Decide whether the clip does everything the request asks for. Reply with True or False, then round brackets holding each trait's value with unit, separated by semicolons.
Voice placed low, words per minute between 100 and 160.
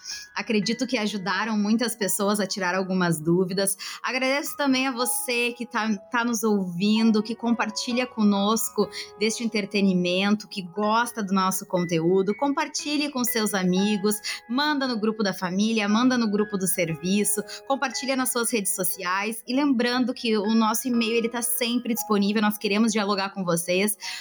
False (215 Hz; 150 wpm)